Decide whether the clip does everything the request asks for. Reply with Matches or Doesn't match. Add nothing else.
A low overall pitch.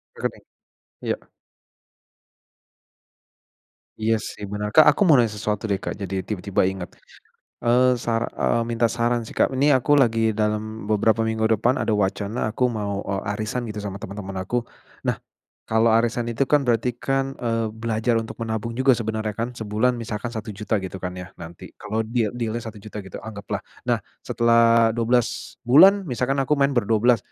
Matches